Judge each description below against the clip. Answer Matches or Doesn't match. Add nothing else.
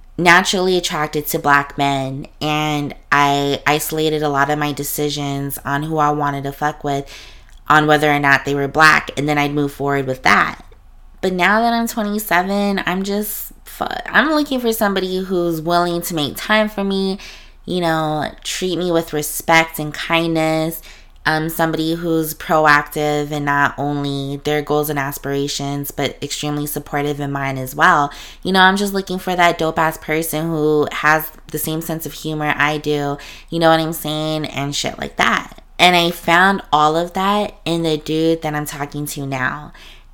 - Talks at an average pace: Matches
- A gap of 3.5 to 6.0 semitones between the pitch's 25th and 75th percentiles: Doesn't match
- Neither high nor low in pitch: Matches